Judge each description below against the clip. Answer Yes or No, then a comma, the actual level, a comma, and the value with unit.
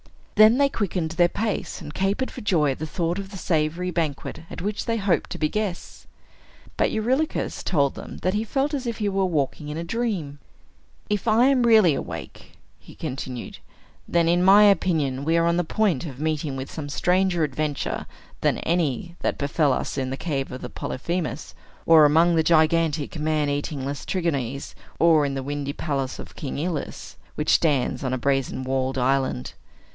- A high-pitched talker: No, medium, 160 Hz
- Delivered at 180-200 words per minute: Yes, average, 185 wpm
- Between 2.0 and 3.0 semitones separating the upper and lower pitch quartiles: No, average, 5.0 semitones